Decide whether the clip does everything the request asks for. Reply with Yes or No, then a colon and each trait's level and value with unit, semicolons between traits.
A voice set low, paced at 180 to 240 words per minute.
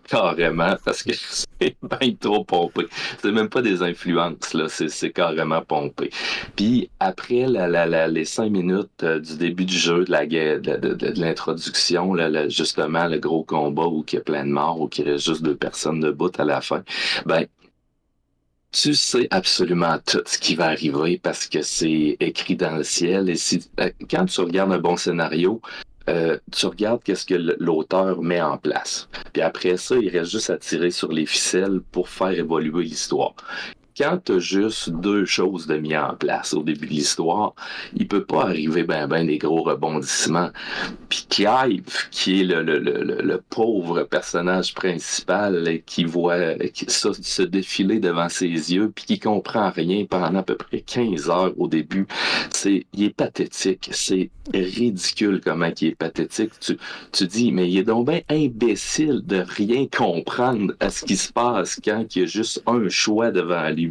Yes: very low, 90 Hz; average, 185 wpm